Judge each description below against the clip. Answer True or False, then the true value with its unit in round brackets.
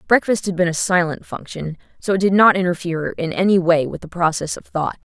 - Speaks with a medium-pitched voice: True (175 Hz)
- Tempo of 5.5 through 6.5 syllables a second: True (5.8 syllables/s)